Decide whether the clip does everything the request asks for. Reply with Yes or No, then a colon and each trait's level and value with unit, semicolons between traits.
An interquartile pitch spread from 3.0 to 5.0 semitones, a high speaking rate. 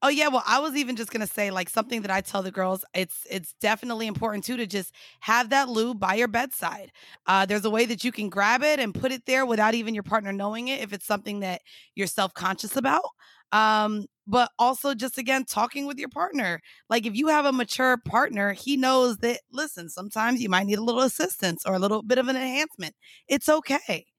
Yes: average, 4.4 semitones; fast, 230 wpm